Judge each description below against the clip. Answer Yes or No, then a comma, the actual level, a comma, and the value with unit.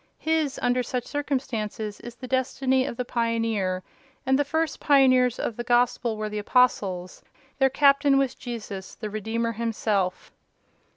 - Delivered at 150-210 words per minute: No, average, 140 wpm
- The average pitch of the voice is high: Yes, high, 240 Hz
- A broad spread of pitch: No, average, 3.6 semitones